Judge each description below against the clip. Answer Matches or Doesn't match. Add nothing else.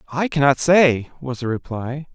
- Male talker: Matches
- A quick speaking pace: Doesn't match